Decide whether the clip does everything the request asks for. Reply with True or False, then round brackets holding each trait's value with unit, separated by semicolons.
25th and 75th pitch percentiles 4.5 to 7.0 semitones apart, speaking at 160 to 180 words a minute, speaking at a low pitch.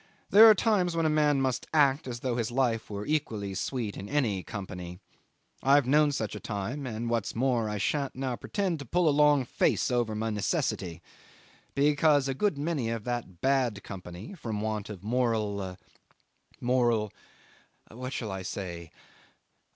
True (5.4 semitones; 165 wpm; 120 Hz)